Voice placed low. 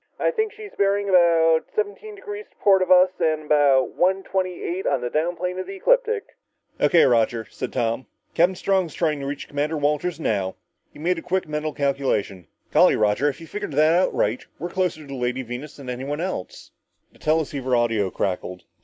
No: medium, 155 Hz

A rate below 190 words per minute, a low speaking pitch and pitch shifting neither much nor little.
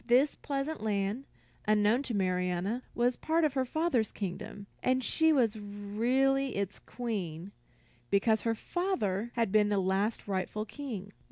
No: average, 145 wpm; high, 220 Hz; average, 4.6 semitones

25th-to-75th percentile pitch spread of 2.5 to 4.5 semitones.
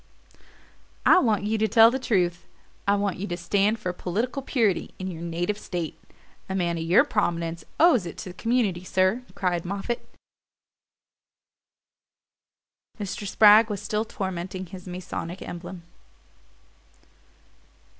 Yes: average, 3.6 semitones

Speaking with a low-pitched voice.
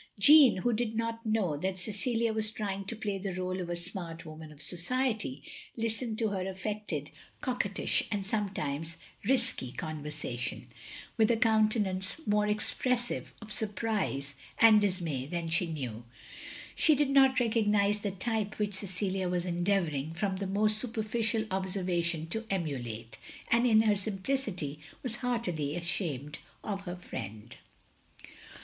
No: high, 200 Hz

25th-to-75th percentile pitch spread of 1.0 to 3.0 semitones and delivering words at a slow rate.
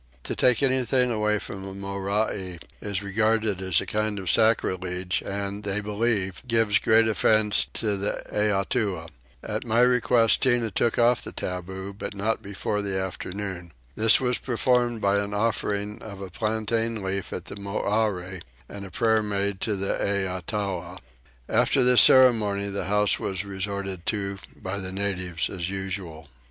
No: narrow, 2.4 semitones; average, 155 wpm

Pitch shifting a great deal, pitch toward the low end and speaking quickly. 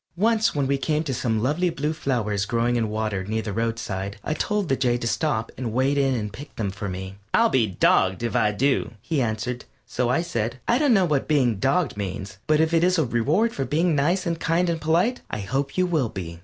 Yes: wide, 6.7 semitones; low, 130 Hz; fast, 235 wpm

